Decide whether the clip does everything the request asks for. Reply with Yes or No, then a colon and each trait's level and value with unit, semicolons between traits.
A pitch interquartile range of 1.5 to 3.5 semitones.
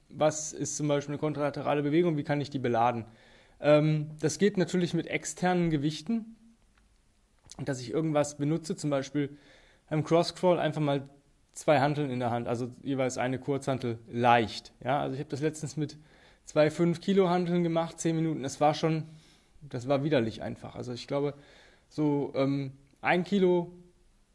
Yes: average, 2.8 semitones